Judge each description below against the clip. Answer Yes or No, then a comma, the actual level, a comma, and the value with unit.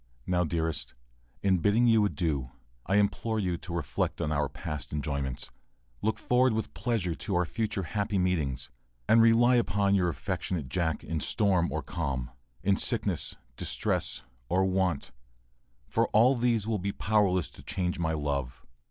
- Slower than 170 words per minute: Yes, average, 160 wpm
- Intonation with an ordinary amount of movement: Yes, average, 4.9 semitones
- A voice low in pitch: Yes, very low, 90 Hz